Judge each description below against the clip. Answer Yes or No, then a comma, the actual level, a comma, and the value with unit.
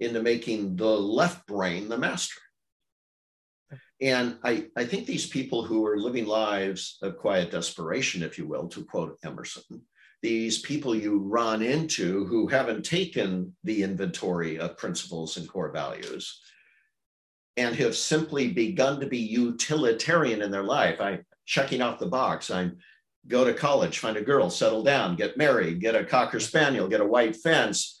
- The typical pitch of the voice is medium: No, low, 110 Hz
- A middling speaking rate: Yes, average, 160 wpm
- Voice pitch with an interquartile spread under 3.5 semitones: No, average, 4.7 semitones